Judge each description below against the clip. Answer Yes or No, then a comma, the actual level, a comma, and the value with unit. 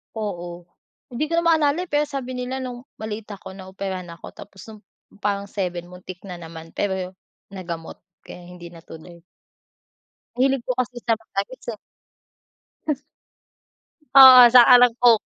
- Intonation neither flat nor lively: No, wide, 5.8 semitones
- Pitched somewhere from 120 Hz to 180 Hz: No, high, 210 Hz